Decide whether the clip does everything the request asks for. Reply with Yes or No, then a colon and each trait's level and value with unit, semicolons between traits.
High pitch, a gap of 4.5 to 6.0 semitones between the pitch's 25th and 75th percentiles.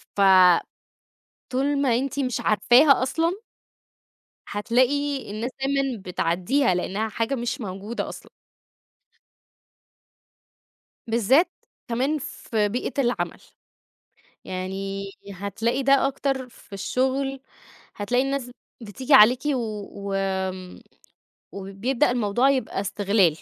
Yes: high, 240 Hz; average, 5.2 semitones